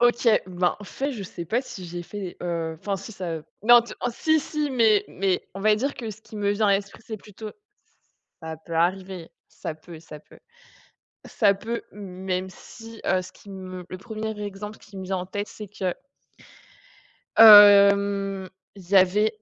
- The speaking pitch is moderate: No, high, 200 Hz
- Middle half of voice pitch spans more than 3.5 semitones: No, average, 2.8 semitones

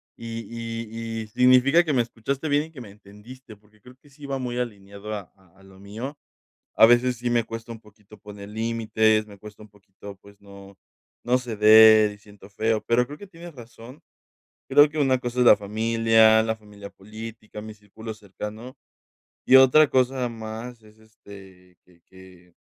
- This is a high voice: No, low, 110 Hz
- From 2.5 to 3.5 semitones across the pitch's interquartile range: Yes, average, 2.9 semitones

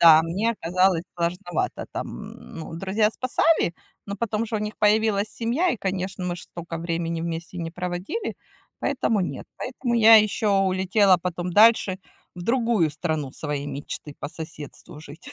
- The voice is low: No, medium, 185 Hz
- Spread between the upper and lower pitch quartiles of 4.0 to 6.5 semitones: Yes, average, 4.5 semitones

